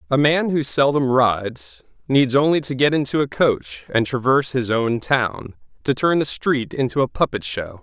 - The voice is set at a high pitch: No, low, 130 Hz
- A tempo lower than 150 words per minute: No, average, 190 wpm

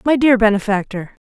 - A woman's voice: Yes, female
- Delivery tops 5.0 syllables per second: Yes, 5.6 syllables/s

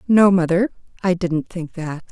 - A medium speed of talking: Yes, average, 170 wpm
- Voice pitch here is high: No, medium, 180 Hz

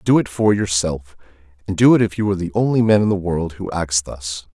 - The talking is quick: Yes, fast, 250 wpm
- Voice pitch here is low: Yes, very low, 95 Hz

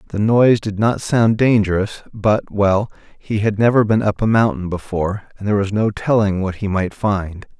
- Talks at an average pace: Yes, average, 190 wpm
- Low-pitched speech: Yes, low, 105 Hz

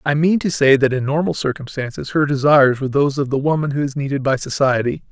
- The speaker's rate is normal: No, fast, 235 wpm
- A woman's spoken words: No, male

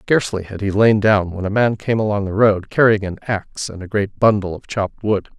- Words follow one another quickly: Yes, fast, 245 wpm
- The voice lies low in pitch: Yes, low, 105 Hz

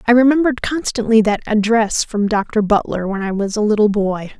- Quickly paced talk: No, average, 190 wpm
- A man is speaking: No, female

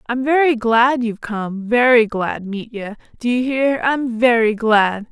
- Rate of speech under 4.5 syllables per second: Yes, 4.0 syllables/s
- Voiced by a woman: Yes, female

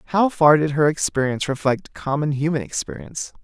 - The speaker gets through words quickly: No, average, 155 wpm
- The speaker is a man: Yes, male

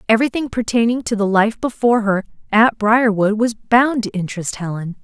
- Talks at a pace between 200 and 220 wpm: No, average, 165 wpm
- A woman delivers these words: Yes, female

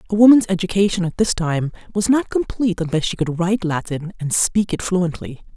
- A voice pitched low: No, medium, 185 Hz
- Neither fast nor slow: Yes, average, 195 wpm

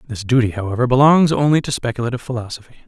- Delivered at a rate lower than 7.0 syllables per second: No, 7.6 syllables/s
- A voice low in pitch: Yes, low, 125 Hz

